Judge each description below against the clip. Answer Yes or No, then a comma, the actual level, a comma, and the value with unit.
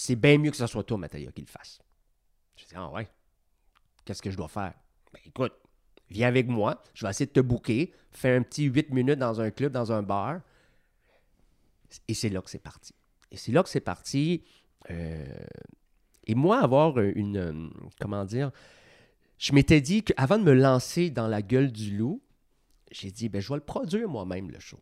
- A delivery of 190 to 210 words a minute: Yes, average, 200 wpm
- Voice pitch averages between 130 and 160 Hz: No, low, 120 Hz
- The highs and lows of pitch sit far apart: Yes, wide, 6.2 semitones